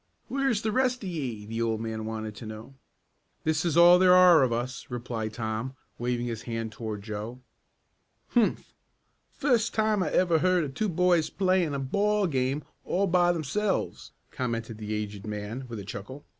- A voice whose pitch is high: No, low, 130 Hz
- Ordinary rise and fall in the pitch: No, wide, 8.4 semitones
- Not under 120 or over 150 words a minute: No, average, 175 wpm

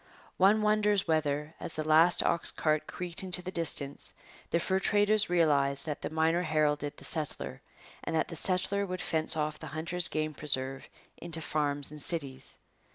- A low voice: No, medium, 160 Hz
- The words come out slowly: No, average, 170 wpm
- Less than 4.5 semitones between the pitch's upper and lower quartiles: Yes, average, 3.1 semitones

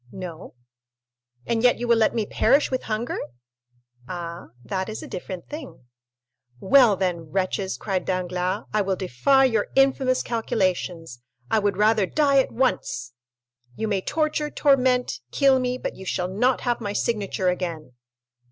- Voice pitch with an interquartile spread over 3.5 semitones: Yes, wide, 5.5 semitones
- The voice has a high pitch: Yes, high, 210 Hz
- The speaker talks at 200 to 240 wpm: No, average, 150 wpm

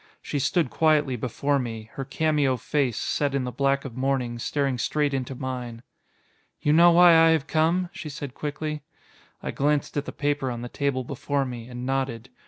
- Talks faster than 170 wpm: Yes, average, 190 wpm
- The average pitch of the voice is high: No, medium, 140 Hz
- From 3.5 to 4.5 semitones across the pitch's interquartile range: No, average, 2.9 semitones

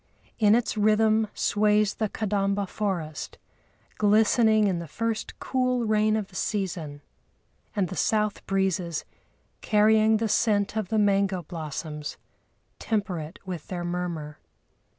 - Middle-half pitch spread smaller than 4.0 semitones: Yes, average, 3.4 semitones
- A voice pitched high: Yes, high, 205 Hz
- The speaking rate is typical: No, slow, 130 wpm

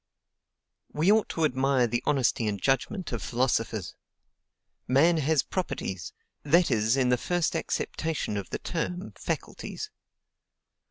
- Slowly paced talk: Yes, slow, 125 wpm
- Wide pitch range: Yes, wide, 6.0 semitones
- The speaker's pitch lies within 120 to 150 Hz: Yes, low, 135 Hz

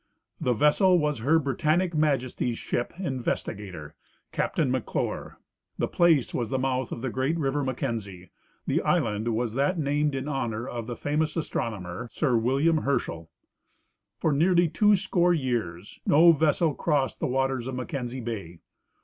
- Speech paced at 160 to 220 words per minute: No, average, 150 wpm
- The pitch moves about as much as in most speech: Yes, average, 4.7 semitones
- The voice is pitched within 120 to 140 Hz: Yes, low, 135 Hz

